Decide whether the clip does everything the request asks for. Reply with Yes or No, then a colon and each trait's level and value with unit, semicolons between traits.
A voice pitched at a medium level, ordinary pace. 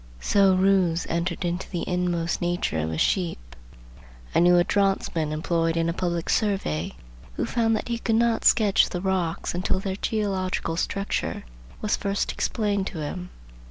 Yes: medium, 180 Hz; average, 160 wpm